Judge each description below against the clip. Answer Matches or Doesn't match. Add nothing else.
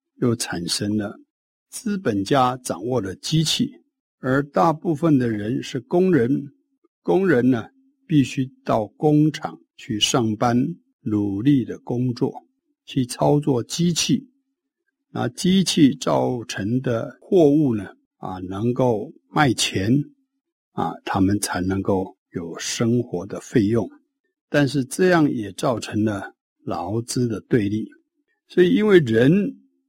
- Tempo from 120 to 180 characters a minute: Matches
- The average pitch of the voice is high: Doesn't match